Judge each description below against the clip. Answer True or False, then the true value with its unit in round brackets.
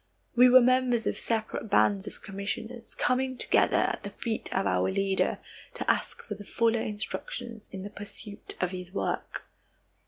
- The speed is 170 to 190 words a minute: False (160 wpm)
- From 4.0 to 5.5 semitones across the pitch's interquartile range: False (3.3 semitones)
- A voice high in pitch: True (215 Hz)